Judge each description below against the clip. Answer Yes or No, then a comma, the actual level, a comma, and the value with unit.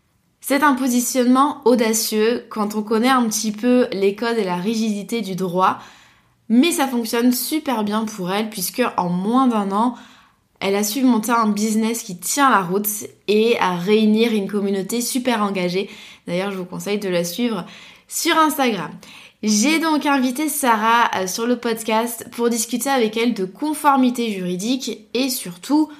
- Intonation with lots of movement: No, average, 3.2 semitones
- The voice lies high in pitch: Yes, high, 225 Hz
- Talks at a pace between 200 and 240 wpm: No, average, 165 wpm